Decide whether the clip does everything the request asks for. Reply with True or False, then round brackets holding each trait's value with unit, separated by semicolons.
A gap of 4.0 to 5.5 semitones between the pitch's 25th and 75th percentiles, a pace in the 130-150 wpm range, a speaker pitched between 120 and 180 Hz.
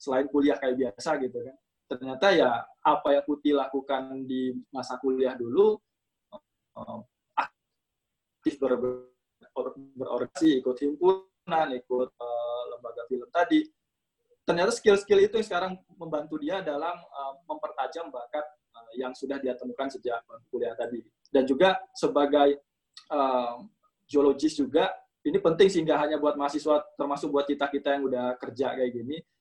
True (5.1 semitones; 135 wpm; 140 Hz)